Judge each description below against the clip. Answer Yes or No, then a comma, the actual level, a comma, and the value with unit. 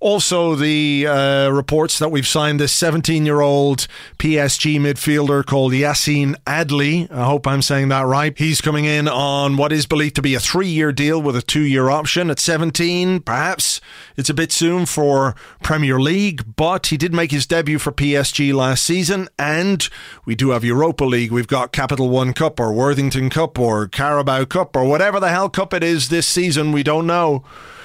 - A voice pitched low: No, medium, 150 Hz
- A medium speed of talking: Yes, average, 190 wpm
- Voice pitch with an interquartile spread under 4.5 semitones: Yes, average, 2.9 semitones